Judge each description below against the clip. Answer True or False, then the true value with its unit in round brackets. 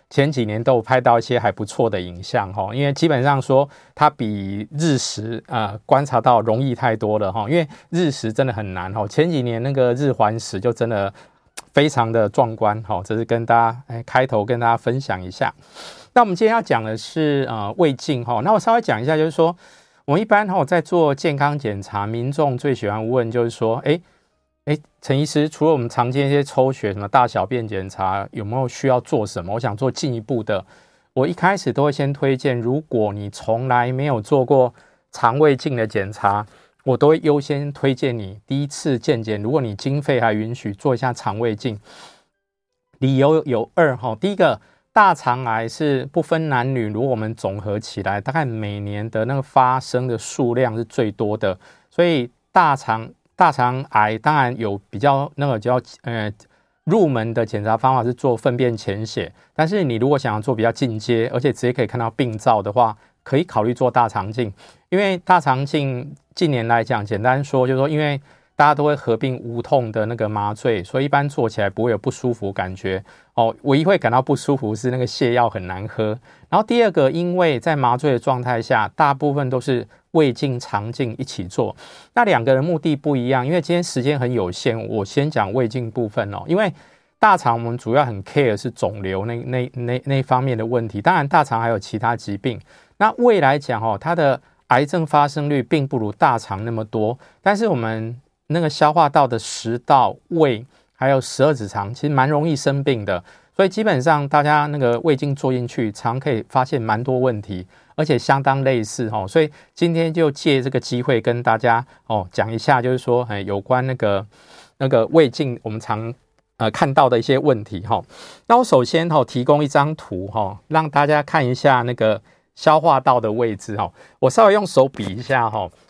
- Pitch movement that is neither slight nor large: True (4.5 semitones)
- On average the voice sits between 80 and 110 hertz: False (125 Hz)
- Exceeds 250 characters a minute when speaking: True (295 characters per minute)